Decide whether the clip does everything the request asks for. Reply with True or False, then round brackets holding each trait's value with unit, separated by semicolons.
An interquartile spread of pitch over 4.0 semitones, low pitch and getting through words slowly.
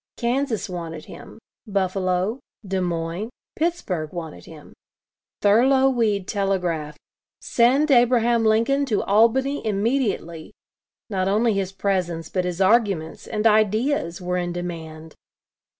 False (4.9 semitones; 200 Hz; 115 wpm)